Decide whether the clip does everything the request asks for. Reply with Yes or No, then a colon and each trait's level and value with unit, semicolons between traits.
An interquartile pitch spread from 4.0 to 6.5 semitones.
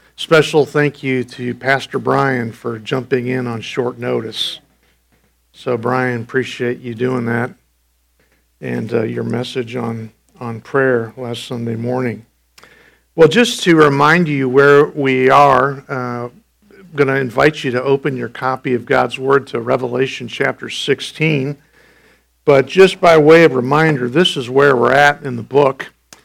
No: average, 2.9 semitones